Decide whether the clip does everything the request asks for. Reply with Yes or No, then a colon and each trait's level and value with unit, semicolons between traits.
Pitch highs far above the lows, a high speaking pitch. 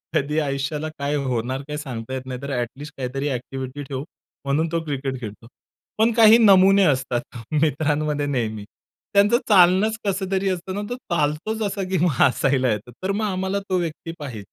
No: wide, 6.1 semitones; medium, 150 Hz